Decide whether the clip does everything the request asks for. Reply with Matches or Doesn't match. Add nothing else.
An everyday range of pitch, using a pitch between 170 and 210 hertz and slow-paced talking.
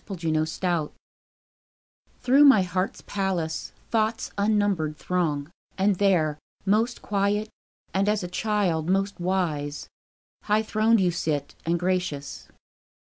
Matches